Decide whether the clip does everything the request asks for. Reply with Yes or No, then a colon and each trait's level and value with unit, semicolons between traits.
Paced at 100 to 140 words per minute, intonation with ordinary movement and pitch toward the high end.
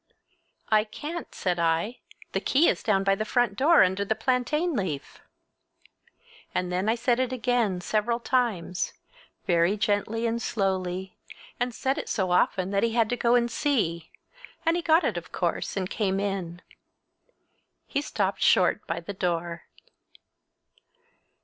No: average, 155 wpm; average, 4.9 semitones; high, 210 Hz